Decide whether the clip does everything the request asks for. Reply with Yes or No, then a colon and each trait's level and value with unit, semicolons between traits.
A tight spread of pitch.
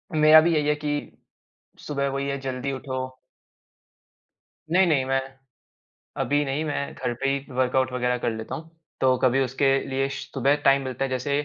Yes: narrow, 1.8 semitones